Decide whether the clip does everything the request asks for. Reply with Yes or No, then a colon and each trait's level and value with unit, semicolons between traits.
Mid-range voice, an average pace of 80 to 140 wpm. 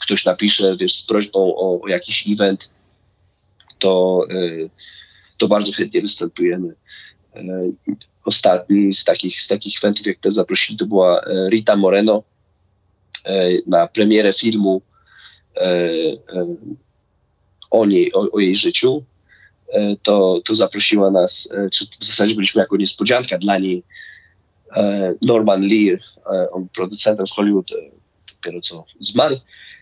No: low, 100 Hz; slow, 110 wpm